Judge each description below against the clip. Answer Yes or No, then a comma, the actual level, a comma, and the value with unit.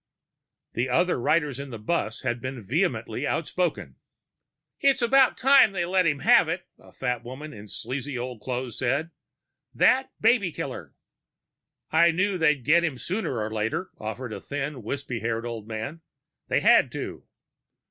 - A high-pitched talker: No, medium, 140 Hz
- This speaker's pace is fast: No, average, 160 wpm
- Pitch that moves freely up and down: Yes, wide, 6.4 semitones